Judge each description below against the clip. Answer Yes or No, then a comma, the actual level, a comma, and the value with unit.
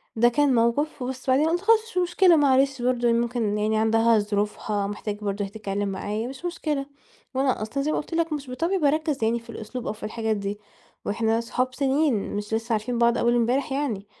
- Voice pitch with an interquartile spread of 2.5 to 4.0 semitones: No, average, 4.4 semitones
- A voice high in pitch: Yes, high, 240 Hz